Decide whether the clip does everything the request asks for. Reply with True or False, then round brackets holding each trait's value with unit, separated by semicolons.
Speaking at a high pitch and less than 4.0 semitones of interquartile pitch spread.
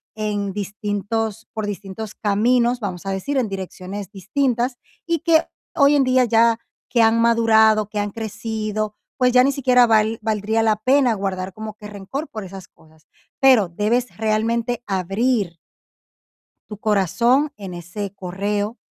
True (215 Hz; 2.9 semitones)